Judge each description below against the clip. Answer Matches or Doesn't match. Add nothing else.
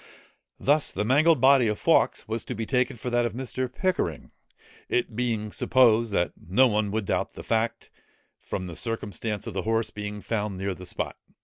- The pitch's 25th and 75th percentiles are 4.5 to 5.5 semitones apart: Doesn't match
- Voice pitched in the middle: Doesn't match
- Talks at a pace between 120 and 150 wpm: Doesn't match